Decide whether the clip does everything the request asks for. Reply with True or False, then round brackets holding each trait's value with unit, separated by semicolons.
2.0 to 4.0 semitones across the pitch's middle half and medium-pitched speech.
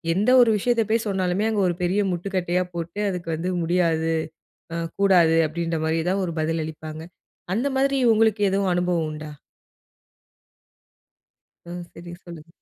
True (3.3 semitones; 175 Hz)